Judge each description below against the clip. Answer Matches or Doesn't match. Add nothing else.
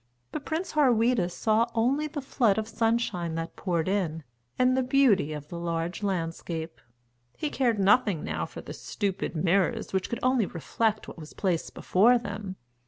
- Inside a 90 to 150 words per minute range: Doesn't match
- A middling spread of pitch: Doesn't match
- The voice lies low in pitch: Doesn't match